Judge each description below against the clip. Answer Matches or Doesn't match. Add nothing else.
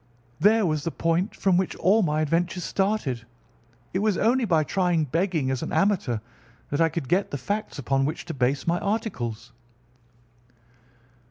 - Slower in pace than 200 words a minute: Matches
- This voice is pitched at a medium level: Matches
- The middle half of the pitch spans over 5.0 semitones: Matches